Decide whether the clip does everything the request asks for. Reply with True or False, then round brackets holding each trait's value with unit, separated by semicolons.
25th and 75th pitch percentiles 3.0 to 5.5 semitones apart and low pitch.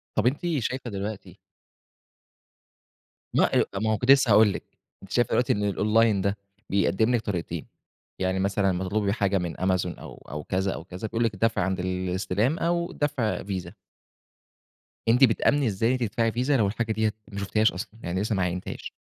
True (3.4 semitones; 105 Hz)